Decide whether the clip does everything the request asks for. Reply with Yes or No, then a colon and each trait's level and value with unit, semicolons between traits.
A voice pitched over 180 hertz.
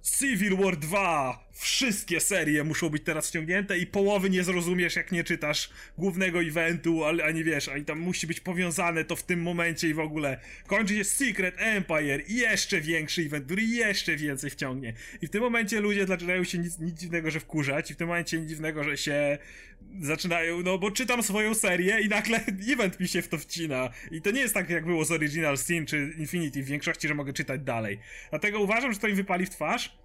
No: medium, 170 Hz